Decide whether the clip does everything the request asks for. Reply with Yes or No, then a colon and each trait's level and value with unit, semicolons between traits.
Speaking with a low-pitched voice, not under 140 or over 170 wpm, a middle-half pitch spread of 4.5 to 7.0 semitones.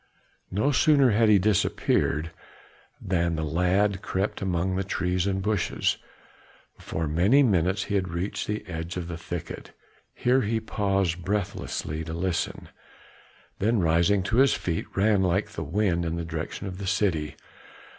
No: very low, 95 Hz; average, 155 wpm; average, 3.4 semitones